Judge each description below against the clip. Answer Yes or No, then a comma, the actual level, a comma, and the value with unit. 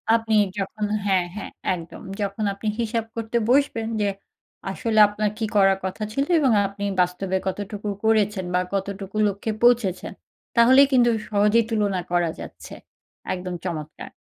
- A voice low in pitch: No, high, 205 Hz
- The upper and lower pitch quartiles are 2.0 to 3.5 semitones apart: Yes, average, 2.8 semitones